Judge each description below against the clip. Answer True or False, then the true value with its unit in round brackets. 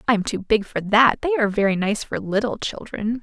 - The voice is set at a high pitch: True (215 Hz)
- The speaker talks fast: True (240 wpm)